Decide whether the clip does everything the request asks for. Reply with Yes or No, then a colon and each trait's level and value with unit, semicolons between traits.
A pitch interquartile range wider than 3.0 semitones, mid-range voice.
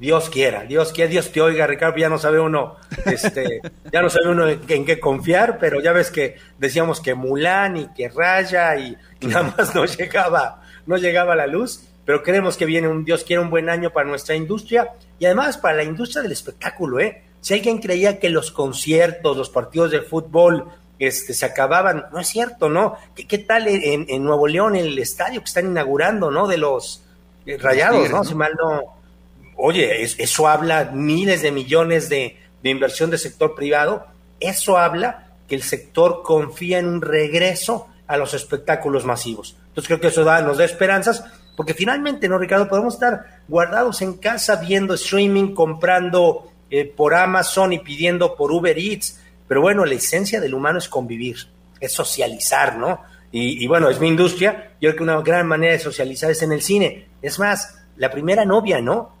Yes: average, 4.2 semitones; medium, 165 Hz